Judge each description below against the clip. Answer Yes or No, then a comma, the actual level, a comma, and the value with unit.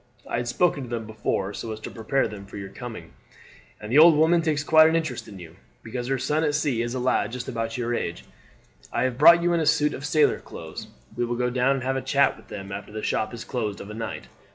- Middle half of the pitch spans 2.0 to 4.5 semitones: No, average, 5.1 semitones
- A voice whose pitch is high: No, low, 125 Hz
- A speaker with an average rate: No, fast, 265 wpm